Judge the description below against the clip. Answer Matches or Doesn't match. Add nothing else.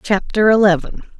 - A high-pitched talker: Matches